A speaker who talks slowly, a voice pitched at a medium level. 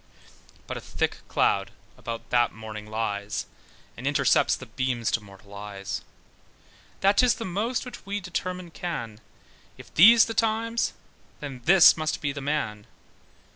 No: average, 145 wpm; medium, 145 Hz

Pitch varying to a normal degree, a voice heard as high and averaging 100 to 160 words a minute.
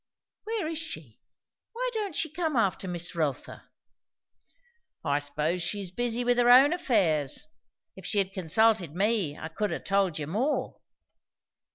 No: wide, 8.1 semitones; high, 200 Hz; average, 150 wpm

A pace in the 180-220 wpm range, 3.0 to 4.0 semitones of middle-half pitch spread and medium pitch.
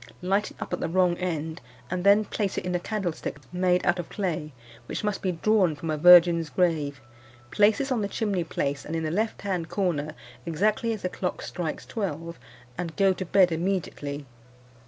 Yes: average, 195 wpm; average, 3.4 semitones; medium, 180 Hz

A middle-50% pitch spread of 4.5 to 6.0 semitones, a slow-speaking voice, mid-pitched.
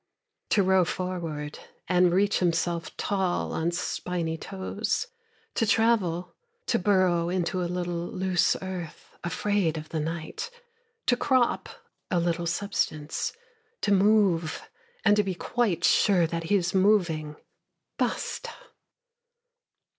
No: average, 2.9 semitones; slow, 120 wpm; medium, 180 Hz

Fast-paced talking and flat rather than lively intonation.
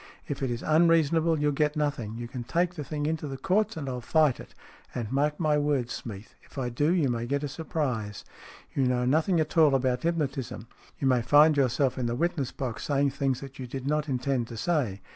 No: fast, 220 wpm; average, 3.6 semitones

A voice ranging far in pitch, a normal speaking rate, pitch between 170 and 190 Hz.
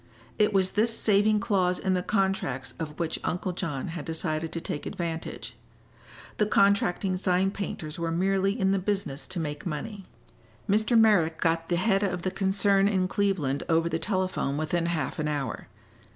No: average, 3.3 semitones; average, 170 wpm; medium, 185 Hz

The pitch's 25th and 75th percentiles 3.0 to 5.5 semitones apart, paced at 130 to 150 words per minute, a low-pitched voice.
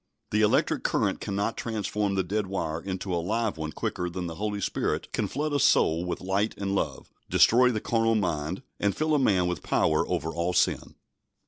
No: average, 3.5 semitones; average, 200 wpm; low, 100 Hz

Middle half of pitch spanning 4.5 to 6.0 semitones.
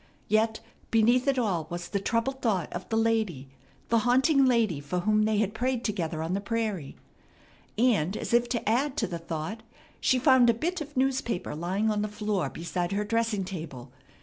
Yes: average, 5.0 semitones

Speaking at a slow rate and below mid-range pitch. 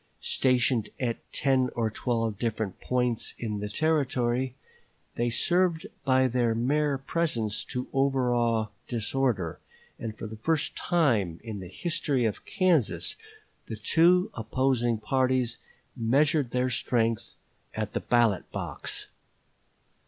Yes: slow, 120 wpm; low, 120 Hz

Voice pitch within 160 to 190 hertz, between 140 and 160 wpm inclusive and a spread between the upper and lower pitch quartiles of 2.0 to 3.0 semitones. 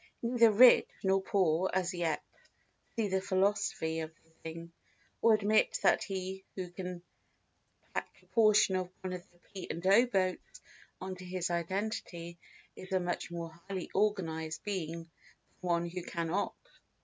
Yes: medium, 185 Hz; average, 155 wpm; narrow, 2.6 semitones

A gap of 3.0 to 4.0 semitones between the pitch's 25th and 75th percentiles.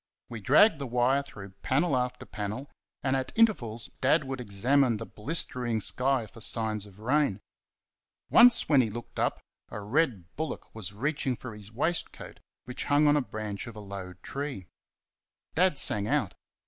No: average, 5.0 semitones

